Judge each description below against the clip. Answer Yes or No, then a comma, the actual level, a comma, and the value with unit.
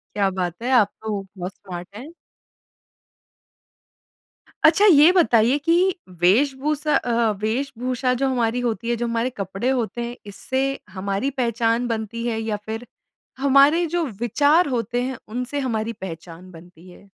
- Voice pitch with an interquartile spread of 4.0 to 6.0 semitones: Yes, average, 4.4 semitones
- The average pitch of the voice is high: Yes, high, 235 Hz